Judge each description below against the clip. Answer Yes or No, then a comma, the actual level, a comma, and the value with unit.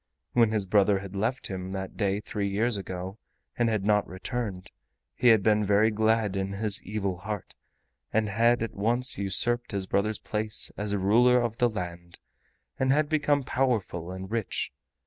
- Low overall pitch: Yes, low, 105 Hz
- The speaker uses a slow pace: No, average, 170 wpm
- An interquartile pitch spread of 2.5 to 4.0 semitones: Yes, average, 3.1 semitones